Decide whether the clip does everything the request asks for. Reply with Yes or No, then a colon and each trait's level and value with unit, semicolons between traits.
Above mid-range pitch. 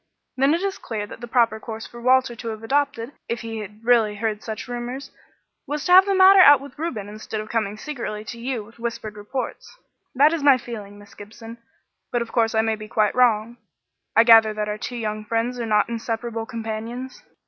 Yes: high, 230 Hz